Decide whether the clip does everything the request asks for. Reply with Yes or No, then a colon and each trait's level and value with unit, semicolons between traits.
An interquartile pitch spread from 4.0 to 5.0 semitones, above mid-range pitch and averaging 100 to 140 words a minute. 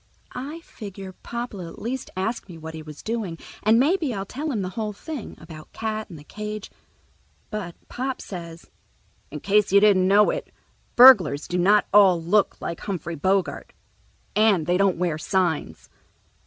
No: average, 4.3 semitones; high, 195 Hz; average, 165 wpm